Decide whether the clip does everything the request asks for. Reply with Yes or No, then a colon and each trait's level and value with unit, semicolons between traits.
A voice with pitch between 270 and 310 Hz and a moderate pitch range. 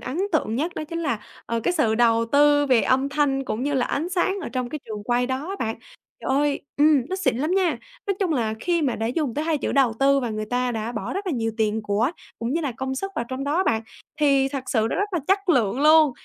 Yes: very high, 275 Hz; average, 4.8 semitones